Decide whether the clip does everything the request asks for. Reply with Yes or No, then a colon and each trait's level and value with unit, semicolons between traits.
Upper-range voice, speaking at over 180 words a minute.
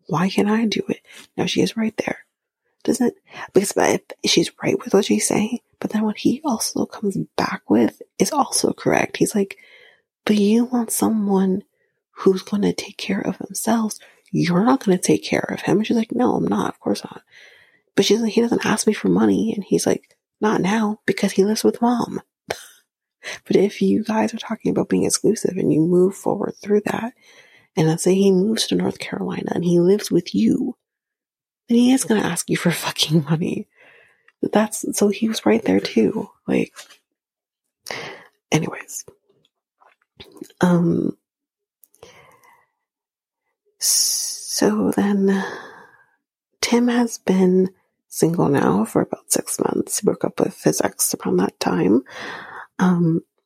No: high, 215 Hz; average, 165 wpm